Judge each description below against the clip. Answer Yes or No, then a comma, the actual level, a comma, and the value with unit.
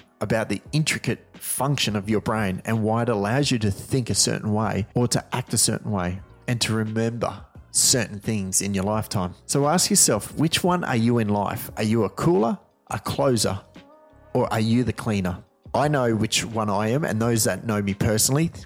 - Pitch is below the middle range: Yes, low, 115 Hz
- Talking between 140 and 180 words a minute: No, fast, 205 wpm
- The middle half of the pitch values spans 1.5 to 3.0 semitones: No, average, 3.4 semitones